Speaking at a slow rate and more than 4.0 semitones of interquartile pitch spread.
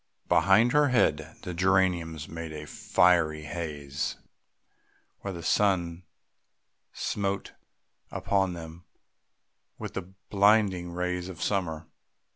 No: slow, 100 wpm; average, 3.1 semitones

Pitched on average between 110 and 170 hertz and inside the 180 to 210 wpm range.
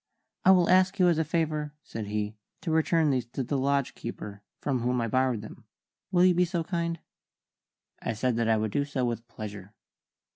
Yes: low, 135 Hz; fast, 205 wpm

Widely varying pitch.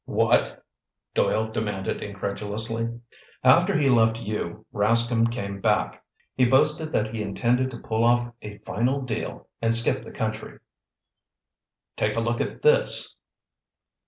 No: average, 2.7 semitones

